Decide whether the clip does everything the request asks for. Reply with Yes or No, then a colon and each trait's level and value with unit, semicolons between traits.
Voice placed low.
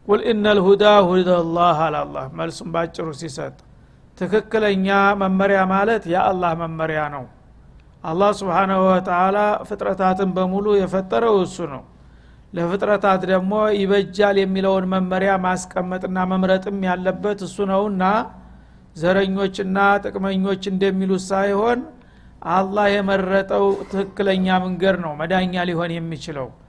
No: high, 190 Hz